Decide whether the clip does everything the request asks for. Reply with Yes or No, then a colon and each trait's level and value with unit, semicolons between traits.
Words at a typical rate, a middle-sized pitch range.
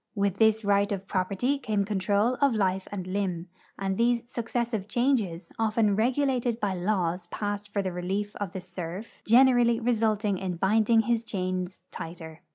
Yes: average, 160 wpm; average, 3.5 semitones